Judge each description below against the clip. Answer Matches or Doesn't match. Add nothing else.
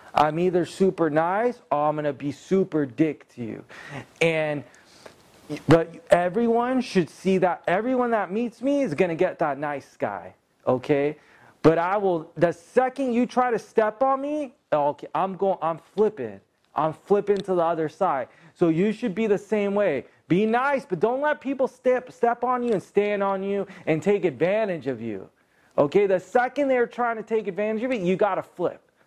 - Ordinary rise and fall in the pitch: Doesn't match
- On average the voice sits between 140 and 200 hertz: Matches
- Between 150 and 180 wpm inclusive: Doesn't match